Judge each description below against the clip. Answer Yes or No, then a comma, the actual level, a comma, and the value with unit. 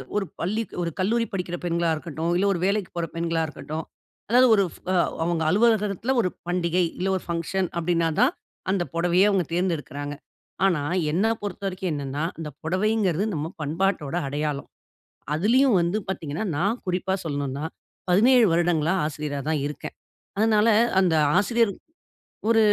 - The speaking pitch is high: No, medium, 175 Hz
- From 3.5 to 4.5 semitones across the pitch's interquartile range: Yes, average, 3.9 semitones